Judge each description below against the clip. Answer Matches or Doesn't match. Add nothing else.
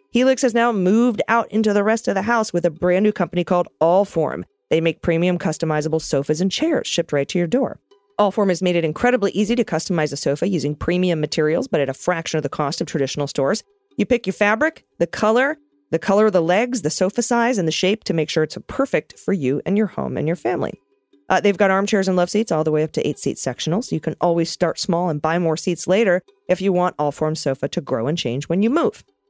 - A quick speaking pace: Matches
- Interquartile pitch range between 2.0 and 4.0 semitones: Doesn't match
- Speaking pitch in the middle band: Matches